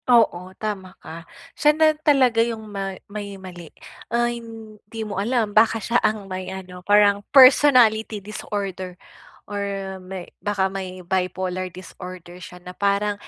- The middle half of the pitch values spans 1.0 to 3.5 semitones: Yes, average, 3.2 semitones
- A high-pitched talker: Yes, high, 200 Hz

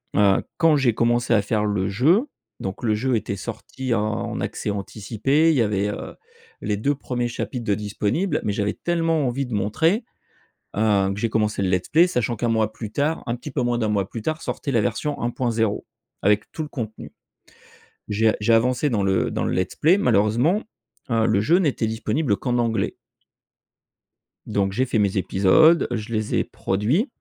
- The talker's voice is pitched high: No, low, 115 Hz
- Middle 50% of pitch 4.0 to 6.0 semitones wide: Yes, average, 4.5 semitones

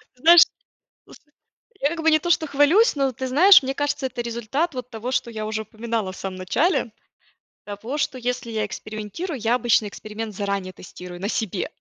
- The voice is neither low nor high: No, high, 240 Hz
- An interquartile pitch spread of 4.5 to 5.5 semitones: Yes, average, 5.2 semitones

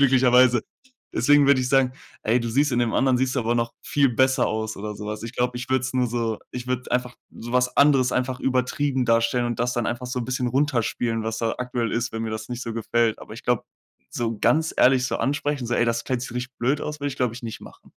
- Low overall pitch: Yes, low, 125 Hz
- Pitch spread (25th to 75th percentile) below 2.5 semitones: Yes, narrow, 1.9 semitones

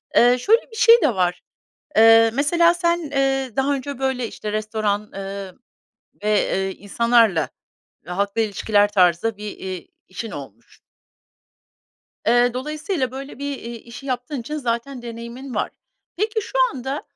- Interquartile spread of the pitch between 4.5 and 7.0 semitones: Yes, average, 5.0 semitones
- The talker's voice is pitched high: Yes, high, 240 Hz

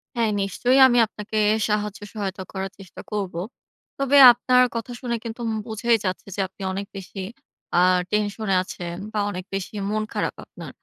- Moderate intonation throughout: Yes, average, 3.1 semitones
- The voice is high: Yes, high, 210 Hz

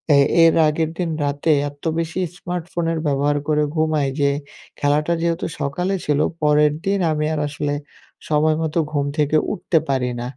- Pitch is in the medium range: Yes, medium, 150 Hz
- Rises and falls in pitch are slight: Yes, narrow, 2.2 semitones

